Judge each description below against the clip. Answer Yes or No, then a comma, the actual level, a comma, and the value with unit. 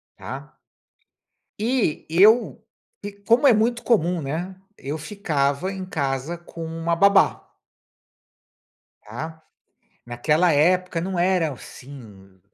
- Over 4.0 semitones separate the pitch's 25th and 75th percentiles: Yes, average, 4.9 semitones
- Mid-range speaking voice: Yes, medium, 165 Hz